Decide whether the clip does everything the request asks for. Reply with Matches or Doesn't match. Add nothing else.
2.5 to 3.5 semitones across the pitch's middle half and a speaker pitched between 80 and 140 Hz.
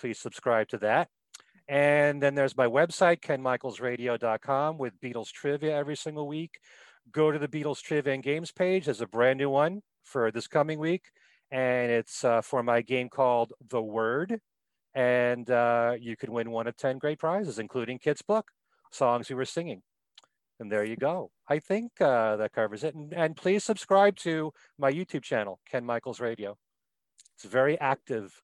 Doesn't match